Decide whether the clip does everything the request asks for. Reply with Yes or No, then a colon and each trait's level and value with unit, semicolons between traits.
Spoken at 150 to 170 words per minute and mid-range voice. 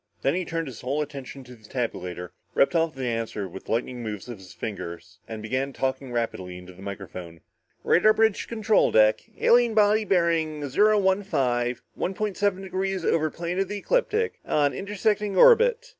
No: average, 185 wpm; medium, 145 Hz